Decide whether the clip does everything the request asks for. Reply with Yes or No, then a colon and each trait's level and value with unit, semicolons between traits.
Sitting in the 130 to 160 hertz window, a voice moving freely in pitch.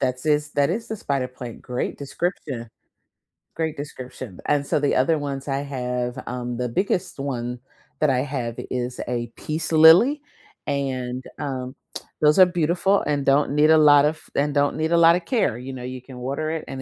No: medium, 140 Hz; average, 3.6 semitones